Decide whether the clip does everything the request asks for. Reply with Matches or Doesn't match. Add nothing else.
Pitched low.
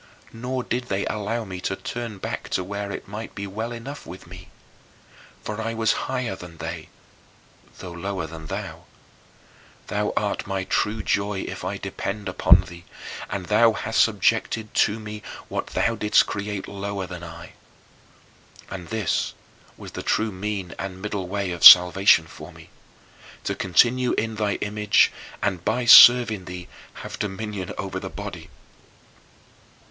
Matches